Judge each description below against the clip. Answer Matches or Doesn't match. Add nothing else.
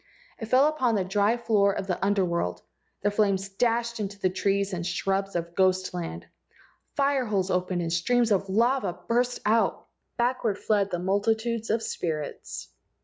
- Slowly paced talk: Doesn't match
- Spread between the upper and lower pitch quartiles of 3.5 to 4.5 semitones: Matches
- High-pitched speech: Matches